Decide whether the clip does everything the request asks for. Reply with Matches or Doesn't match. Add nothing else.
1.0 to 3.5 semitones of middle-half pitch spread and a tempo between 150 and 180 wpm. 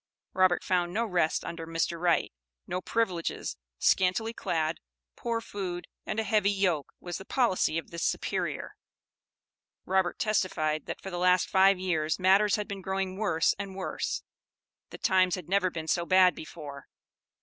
Matches